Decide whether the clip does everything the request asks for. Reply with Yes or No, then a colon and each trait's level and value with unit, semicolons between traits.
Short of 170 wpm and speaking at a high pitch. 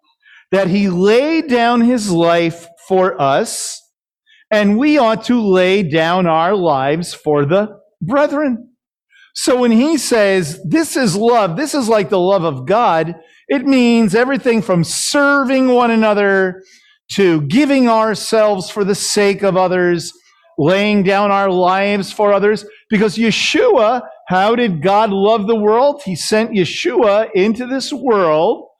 Yes: average, 140 wpm; high, 210 Hz